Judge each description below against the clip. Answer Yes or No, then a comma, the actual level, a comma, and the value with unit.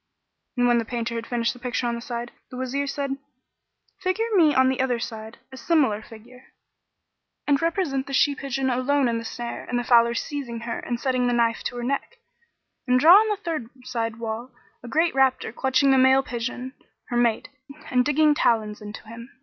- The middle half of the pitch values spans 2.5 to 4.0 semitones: Yes, average, 2.8 semitones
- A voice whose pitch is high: Yes, very high, 250 Hz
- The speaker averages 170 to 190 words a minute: No, average, 200 wpm